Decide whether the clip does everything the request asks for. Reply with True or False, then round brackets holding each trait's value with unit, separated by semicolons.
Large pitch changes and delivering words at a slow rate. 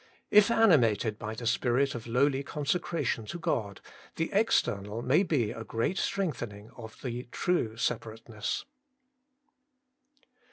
True (6.5 semitones; 120 wpm)